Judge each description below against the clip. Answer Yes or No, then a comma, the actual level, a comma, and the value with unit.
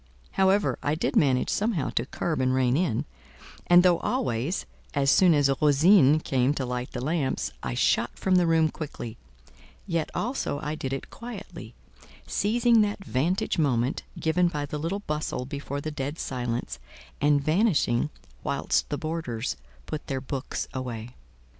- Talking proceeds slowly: No, average, 155 wpm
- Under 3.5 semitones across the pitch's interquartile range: No, average, 5.2 semitones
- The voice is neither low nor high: Yes, medium, 150 Hz